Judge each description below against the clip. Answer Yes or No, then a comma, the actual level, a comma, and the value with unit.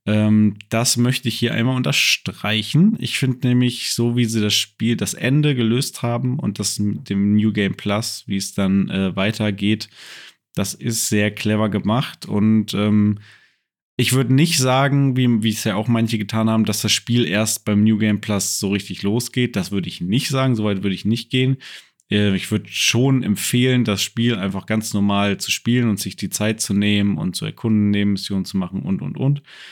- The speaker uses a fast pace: Yes, fast, 200 wpm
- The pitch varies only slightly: No, average, 3.2 semitones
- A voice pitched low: Yes, low, 110 Hz